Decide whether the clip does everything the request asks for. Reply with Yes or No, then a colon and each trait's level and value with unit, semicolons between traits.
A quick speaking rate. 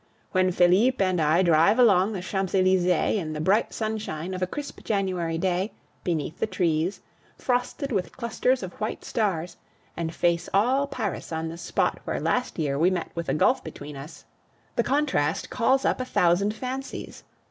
No: average, 175 wpm